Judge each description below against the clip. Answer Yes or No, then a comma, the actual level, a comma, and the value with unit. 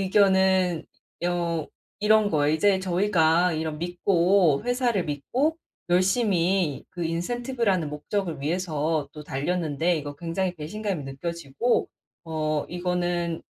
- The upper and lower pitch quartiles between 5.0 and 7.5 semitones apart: No, average, 3.5 semitones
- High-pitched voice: No, medium, 175 Hz